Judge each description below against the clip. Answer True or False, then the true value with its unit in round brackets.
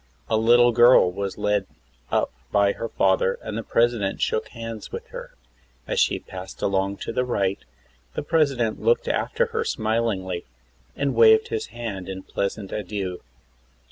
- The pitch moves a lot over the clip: False (3.5 semitones)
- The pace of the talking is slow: False (160 wpm)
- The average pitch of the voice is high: False (110 Hz)